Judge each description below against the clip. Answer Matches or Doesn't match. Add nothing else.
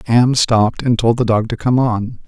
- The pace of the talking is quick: Matches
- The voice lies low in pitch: Matches